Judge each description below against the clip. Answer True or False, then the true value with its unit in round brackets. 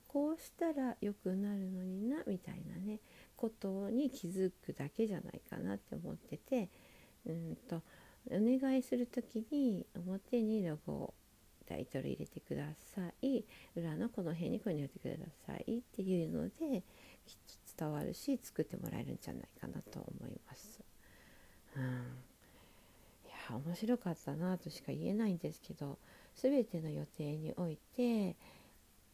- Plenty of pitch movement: True (6.5 semitones)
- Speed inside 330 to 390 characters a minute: False (290 characters per minute)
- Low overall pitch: False (190 Hz)